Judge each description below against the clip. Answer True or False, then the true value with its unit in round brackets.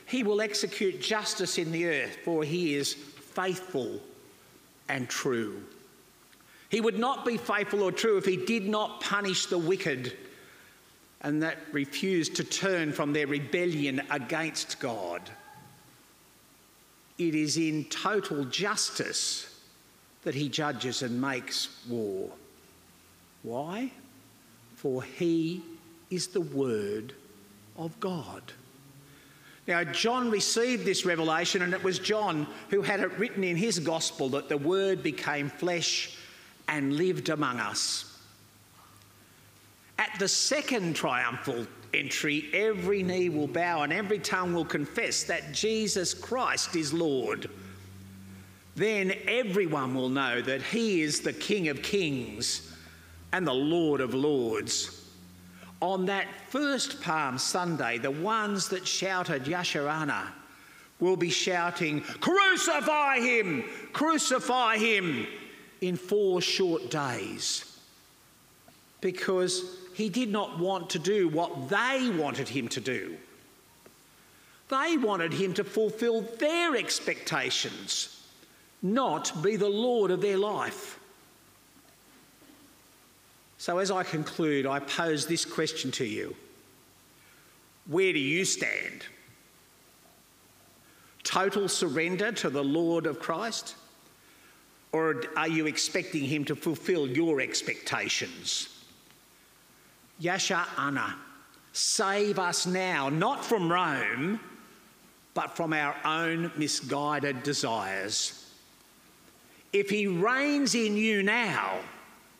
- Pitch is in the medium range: True (175 Hz)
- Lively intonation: True (5.9 semitones)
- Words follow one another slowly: True (115 wpm)